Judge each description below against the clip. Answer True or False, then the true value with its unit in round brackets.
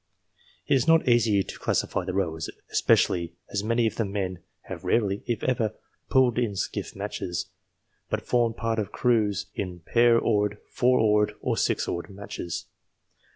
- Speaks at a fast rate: False (160 wpm)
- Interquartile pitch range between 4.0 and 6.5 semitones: False (3.5 semitones)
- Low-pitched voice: True (105 Hz)